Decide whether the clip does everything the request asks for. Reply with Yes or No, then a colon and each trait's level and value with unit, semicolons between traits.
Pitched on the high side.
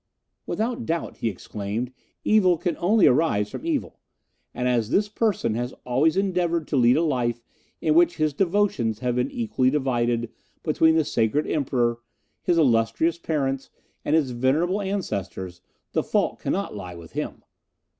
No: medium, 140 Hz